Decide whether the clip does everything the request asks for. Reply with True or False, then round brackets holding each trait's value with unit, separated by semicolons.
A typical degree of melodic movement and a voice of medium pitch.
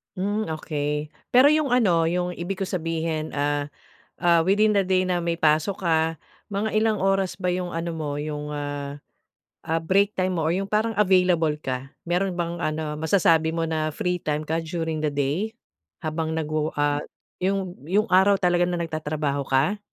True (3.4 semitones; 165 Hz)